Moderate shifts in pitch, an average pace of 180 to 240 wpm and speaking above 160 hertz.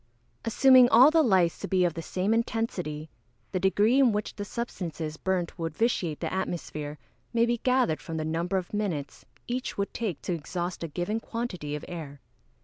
No: wide, 5.8 semitones; average, 190 wpm; medium, 185 Hz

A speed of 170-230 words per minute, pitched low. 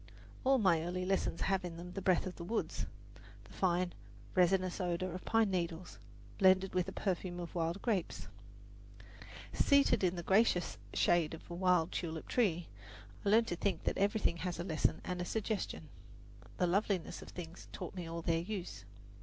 No: average, 180 wpm; medium, 180 Hz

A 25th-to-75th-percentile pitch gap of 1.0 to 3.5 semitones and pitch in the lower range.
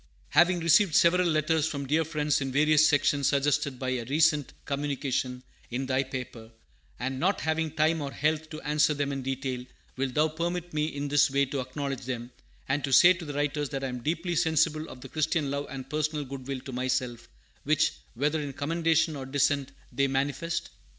No: average, 2.7 semitones; medium, 145 Hz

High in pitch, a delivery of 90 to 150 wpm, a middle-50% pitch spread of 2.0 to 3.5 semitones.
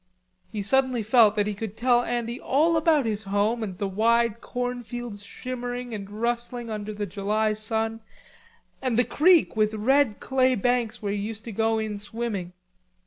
No: high, 225 Hz; average, 175 wpm; average, 2.7 semitones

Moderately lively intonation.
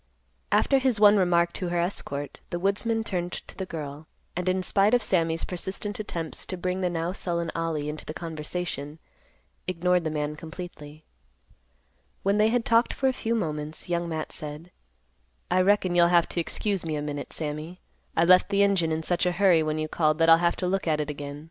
Yes: average, 3.3 semitones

